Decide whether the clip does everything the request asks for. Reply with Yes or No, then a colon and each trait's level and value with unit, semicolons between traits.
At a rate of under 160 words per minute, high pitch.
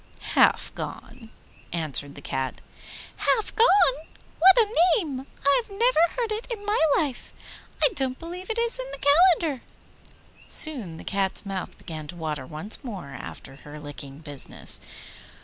Yes: average, 150 wpm; very high, 260 Hz